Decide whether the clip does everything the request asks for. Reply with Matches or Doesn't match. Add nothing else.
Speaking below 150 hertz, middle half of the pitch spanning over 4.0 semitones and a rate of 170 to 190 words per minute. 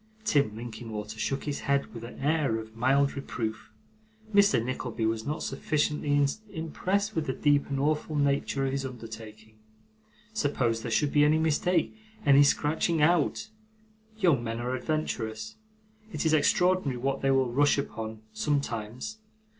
Doesn't match